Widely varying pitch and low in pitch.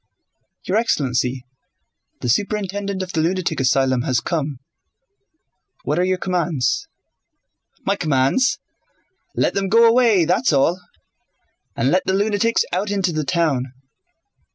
No: wide, 6.6 semitones; medium, 180 Hz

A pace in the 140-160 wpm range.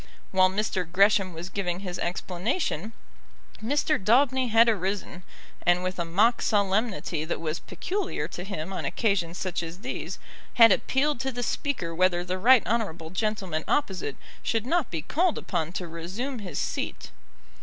Yes: average, 155 wpm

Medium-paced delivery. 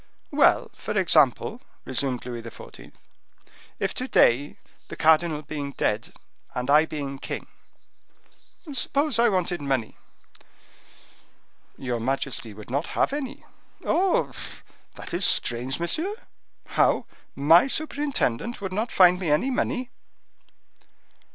No: slow, 115 wpm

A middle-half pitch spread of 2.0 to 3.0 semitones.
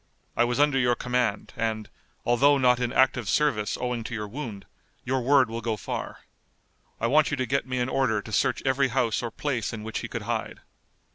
Yes: average, 2.7 semitones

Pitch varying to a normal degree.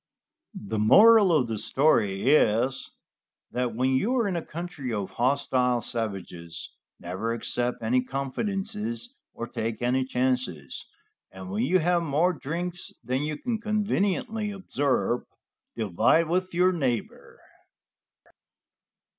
No: wide, 7.5 semitones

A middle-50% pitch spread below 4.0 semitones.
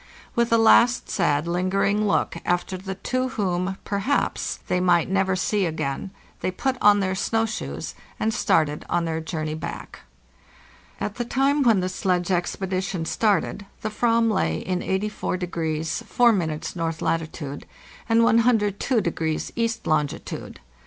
No: average, 4.8 semitones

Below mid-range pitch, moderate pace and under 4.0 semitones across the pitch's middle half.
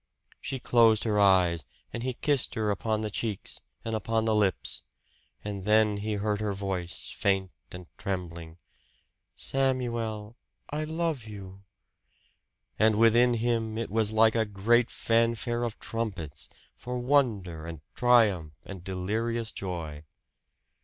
No: low, 110 Hz; slow, 130 wpm; average, 3.3 semitones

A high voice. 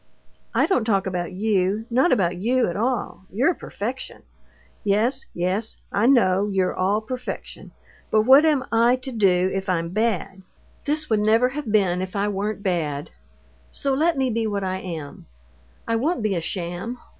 Yes: high, 210 Hz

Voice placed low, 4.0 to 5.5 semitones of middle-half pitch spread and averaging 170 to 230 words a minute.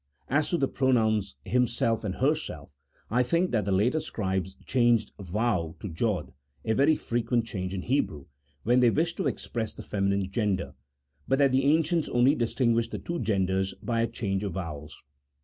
Yes: low, 115 Hz; average, 5.2 semitones; average, 180 wpm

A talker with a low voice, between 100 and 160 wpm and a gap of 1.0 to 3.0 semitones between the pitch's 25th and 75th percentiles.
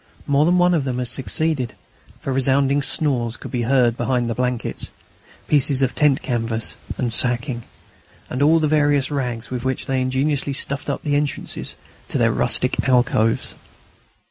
No: low, 130 Hz; average, 170 wpm; average, 2.7 semitones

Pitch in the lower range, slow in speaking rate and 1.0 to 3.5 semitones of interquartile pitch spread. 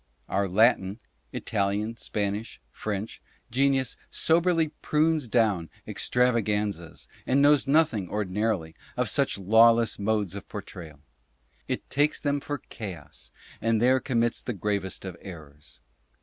No: low, 110 Hz; slow, 120 wpm; average, 4.8 semitones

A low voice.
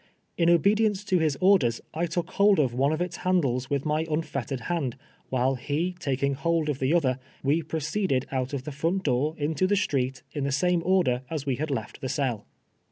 No: medium, 150 Hz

